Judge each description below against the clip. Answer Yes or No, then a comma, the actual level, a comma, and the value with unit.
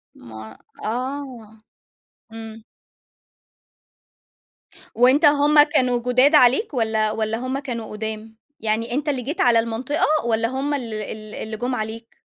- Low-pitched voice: No, high, 235 Hz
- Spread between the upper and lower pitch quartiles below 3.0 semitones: No, average, 3.3 semitones